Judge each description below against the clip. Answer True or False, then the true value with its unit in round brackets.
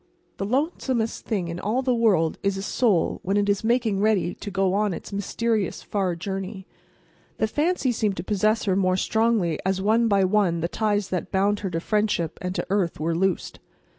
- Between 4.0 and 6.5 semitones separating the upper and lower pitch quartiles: False (2.9 semitones)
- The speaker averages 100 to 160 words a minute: False (195 wpm)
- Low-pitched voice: False (200 Hz)